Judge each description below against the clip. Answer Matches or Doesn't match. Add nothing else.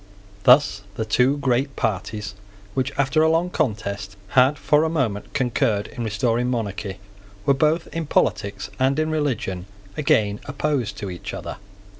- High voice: Doesn't match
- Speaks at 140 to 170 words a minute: Matches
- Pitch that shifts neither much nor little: Doesn't match